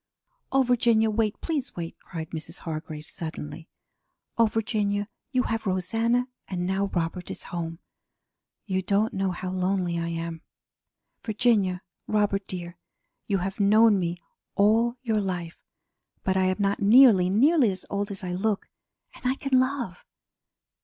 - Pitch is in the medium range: No, high, 195 Hz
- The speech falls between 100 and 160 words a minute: Yes, average, 145 wpm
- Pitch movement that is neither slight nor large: Yes, average, 3.8 semitones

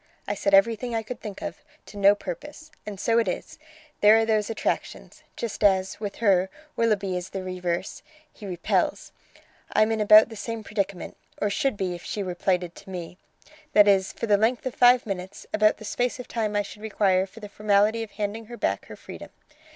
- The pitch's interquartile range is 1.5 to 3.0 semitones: Yes, average, 2.7 semitones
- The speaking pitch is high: Yes, high, 205 Hz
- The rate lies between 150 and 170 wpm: No, fast, 205 wpm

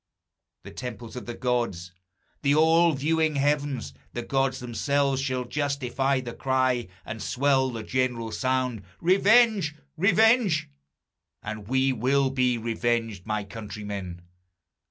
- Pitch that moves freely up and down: No, average, 3.6 semitones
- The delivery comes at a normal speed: No, slow, 120 wpm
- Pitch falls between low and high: No, low, 130 Hz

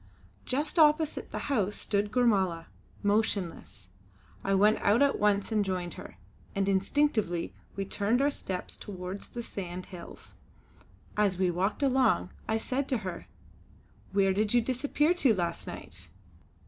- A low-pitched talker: No, high, 205 Hz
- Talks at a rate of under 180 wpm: Yes, average, 145 wpm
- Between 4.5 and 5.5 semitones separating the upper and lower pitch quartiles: Yes, average, 4.9 semitones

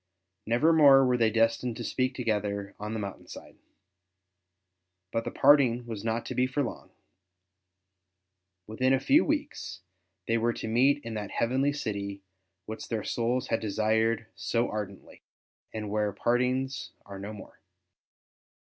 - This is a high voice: No, low, 115 Hz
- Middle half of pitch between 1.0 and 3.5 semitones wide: Yes, average, 3.2 semitones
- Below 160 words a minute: Yes, average, 150 wpm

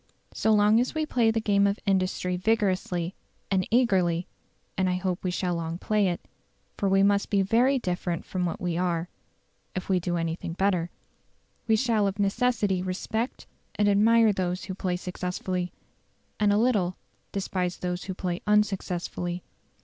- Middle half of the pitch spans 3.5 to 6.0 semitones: No, average, 2.7 semitones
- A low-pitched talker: No, high, 190 Hz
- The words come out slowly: No, average, 165 wpm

